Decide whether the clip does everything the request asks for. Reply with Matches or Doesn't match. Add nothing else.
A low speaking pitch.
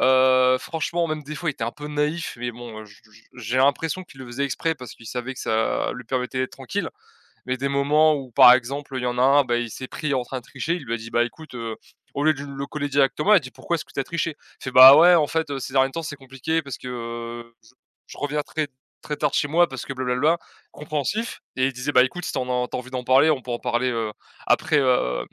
Matches